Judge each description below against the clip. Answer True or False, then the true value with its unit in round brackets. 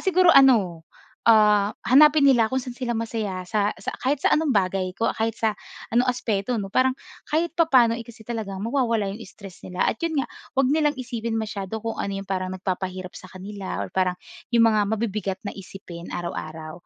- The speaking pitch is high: True (220 Hz)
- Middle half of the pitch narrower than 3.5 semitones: False (4.5 semitones)